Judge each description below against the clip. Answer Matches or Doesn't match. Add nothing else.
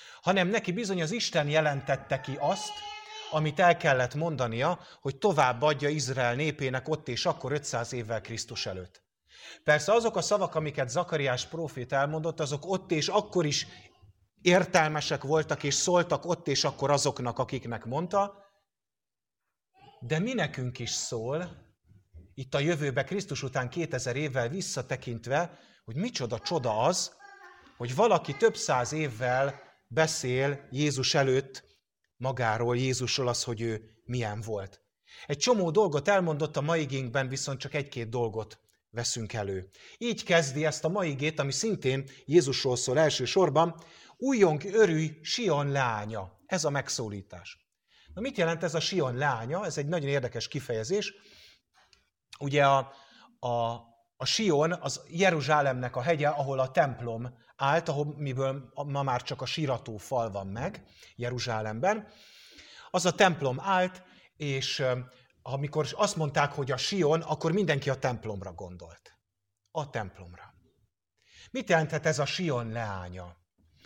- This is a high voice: Doesn't match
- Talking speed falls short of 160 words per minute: Matches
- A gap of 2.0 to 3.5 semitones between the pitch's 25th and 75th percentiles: Doesn't match